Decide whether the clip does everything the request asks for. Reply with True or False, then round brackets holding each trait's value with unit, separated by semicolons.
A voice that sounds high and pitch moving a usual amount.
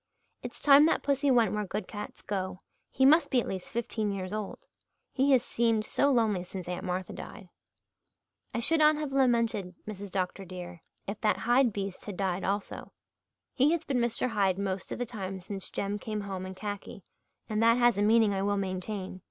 True (210 Hz; 4.0 semitones)